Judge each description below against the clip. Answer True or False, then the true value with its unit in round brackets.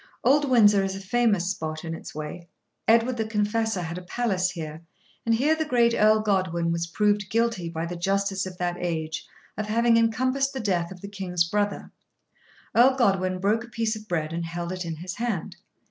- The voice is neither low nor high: False (195 Hz)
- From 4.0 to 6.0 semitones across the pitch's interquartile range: True (4.7 semitones)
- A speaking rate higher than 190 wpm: True (200 wpm)